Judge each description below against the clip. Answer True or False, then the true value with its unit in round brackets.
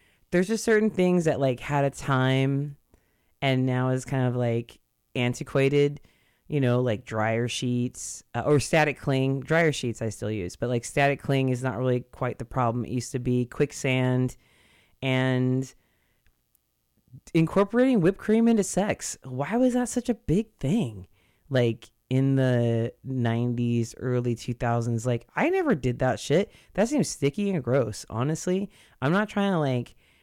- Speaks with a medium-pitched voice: False (130 Hz)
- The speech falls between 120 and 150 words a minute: False (160 wpm)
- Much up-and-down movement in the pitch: False (4.0 semitones)